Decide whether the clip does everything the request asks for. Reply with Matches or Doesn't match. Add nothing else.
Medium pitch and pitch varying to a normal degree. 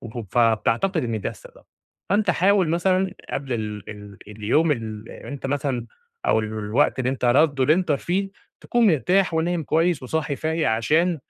Doesn't match